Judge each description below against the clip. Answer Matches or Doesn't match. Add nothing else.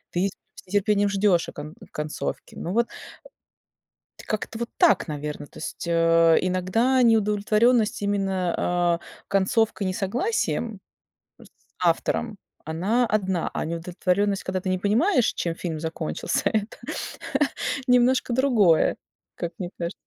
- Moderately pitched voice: Doesn't match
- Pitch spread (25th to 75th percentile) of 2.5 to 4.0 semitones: Doesn't match